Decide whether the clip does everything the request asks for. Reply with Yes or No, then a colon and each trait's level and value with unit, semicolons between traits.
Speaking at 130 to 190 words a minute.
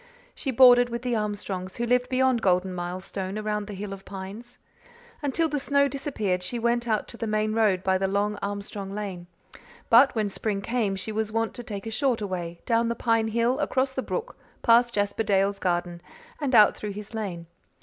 No: average, 200 wpm